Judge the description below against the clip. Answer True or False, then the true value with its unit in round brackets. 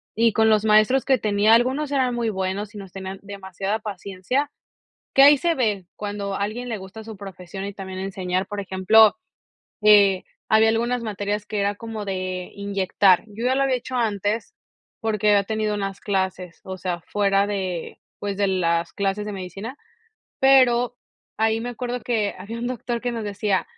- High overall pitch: True (205 Hz)